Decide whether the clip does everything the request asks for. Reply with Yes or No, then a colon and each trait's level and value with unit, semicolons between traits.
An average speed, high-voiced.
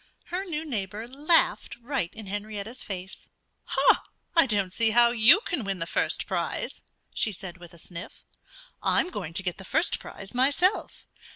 Yes: average, 165 wpm; high, 220 Hz